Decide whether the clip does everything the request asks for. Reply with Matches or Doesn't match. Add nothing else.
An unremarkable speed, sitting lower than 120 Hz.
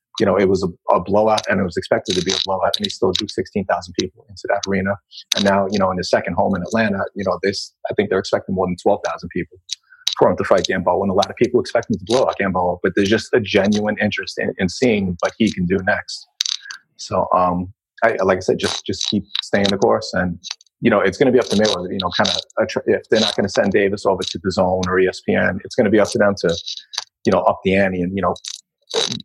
Doesn't match